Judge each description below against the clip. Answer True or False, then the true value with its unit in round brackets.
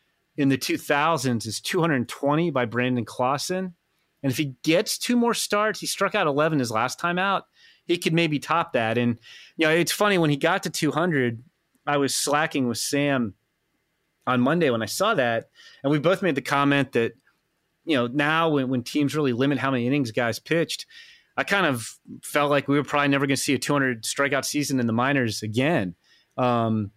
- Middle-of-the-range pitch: True (145 Hz)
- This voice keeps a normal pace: False (215 wpm)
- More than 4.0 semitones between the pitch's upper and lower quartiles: True (4.7 semitones)